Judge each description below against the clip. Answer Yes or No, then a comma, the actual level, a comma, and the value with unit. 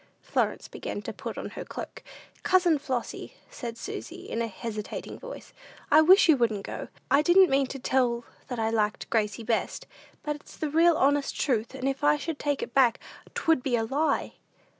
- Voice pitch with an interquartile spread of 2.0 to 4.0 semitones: No, average, 4.5 semitones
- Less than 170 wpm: No, average, 190 wpm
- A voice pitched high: Yes, very high, 270 Hz